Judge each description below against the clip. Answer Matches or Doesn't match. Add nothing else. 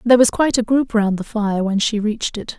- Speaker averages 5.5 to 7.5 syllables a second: Matches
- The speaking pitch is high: Matches